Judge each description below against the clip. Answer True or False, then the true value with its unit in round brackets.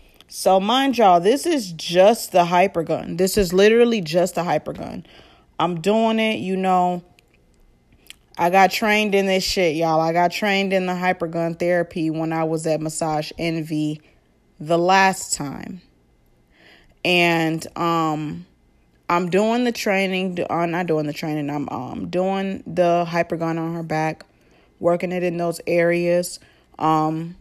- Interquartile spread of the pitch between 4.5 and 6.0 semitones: False (2.9 semitones)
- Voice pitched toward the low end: False (175 Hz)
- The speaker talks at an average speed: True (160 wpm)